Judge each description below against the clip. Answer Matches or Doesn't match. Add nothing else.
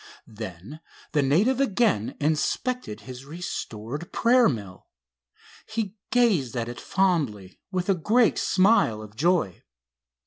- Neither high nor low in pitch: Matches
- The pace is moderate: Doesn't match